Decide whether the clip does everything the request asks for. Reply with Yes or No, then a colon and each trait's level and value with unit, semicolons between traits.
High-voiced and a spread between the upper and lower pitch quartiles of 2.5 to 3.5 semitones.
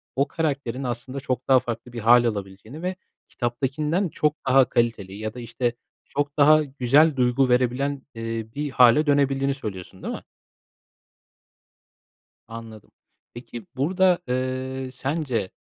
No: low, 130 Hz; average, 3.2 semitones